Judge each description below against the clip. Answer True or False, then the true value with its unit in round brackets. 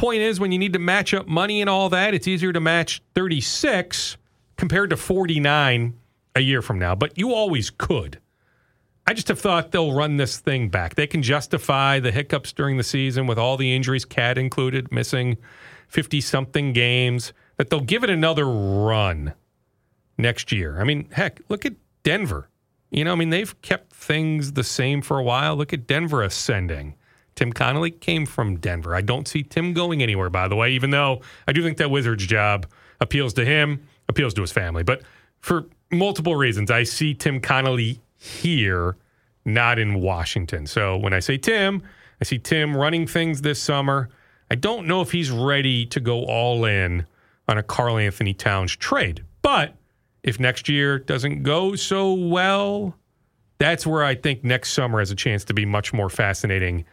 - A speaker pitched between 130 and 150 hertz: True (135 Hz)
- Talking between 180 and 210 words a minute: True (185 wpm)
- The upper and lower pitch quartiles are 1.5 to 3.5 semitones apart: False (5.4 semitones)